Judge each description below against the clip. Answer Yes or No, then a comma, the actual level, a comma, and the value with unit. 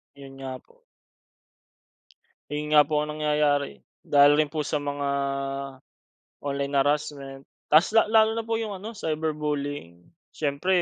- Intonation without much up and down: Yes, narrow, 1.7 semitones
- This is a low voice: No, medium, 150 Hz